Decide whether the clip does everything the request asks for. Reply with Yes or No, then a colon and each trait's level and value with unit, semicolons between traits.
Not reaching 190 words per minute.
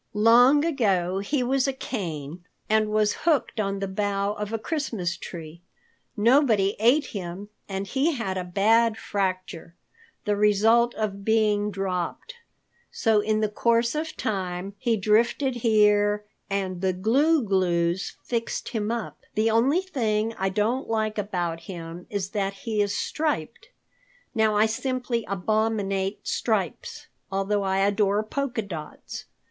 Yes: average, 140 wpm